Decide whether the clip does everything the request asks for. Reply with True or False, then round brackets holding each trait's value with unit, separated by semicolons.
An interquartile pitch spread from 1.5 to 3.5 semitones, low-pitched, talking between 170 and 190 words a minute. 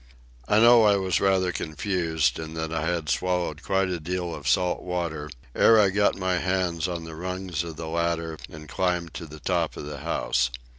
False (2.5 semitones; 85 Hz; 200 wpm)